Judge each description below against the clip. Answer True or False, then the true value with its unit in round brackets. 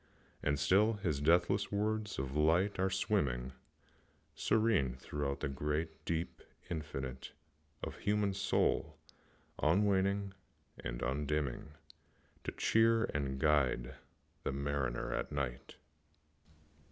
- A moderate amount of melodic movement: False (6.2 semitones)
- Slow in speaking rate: True (105 wpm)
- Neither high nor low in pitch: False (75 Hz)